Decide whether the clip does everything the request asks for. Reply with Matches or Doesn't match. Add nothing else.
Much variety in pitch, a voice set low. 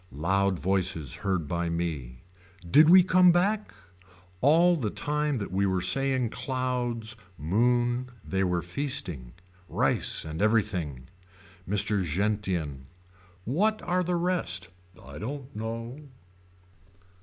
Matches